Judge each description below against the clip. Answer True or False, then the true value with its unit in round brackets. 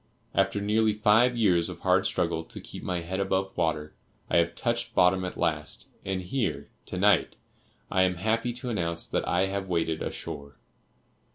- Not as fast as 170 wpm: False (175 wpm)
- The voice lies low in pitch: True (95 Hz)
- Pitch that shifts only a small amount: False (3.8 semitones)